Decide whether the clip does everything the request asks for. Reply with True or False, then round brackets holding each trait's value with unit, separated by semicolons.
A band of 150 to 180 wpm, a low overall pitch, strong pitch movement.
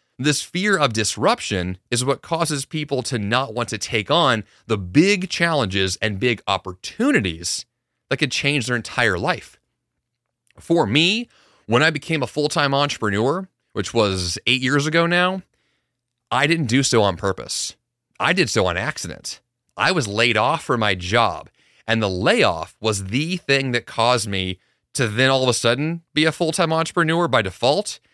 True (175 wpm; 125 Hz; 5.8 semitones)